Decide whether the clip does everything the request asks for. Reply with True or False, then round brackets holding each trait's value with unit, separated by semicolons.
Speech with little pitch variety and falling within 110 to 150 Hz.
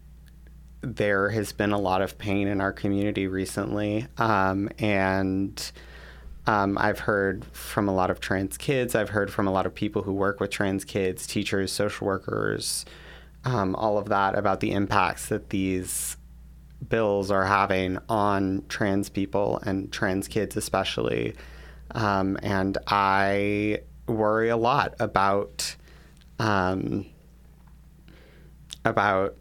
False (1.6 semitones; 100 Hz)